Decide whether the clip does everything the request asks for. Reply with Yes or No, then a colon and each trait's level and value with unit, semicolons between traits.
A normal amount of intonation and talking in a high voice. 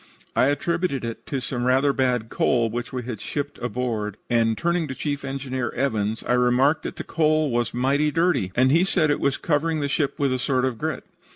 No: average, 3.2 semitones; low, 130 Hz